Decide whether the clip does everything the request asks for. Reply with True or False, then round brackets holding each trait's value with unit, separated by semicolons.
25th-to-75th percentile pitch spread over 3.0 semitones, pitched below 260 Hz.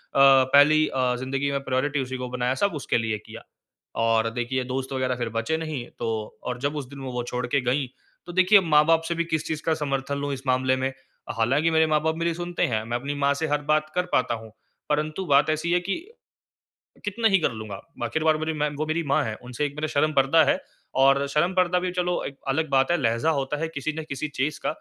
True (3.5 semitones; 140 Hz)